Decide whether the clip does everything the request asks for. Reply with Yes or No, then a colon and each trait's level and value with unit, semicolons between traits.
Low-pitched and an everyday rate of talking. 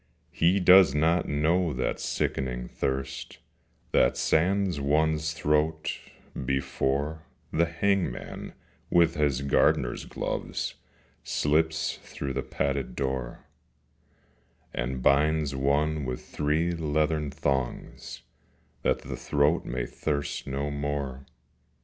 No: very low, 75 Hz; slow, 100 wpm